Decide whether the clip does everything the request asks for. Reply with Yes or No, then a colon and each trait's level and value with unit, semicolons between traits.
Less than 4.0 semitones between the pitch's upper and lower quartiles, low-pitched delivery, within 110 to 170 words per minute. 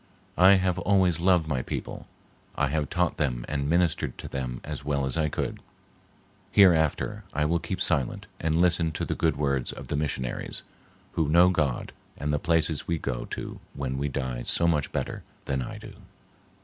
No: average, 3.6 semitones; very low, 75 Hz; average, 185 wpm